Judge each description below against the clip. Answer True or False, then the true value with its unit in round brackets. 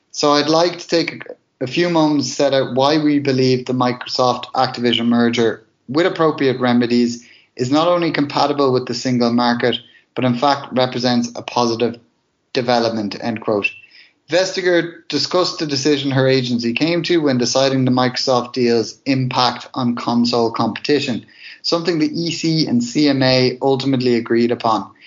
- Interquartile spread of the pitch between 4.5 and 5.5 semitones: False (3.7 semitones)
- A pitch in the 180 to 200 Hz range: False (130 Hz)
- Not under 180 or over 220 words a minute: False (150 wpm)